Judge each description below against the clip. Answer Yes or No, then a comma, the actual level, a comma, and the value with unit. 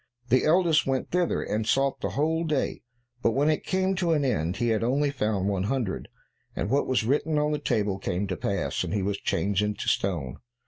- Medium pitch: No, low, 125 Hz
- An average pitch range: No, wide, 6.7 semitones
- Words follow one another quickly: Yes, fast, 215 wpm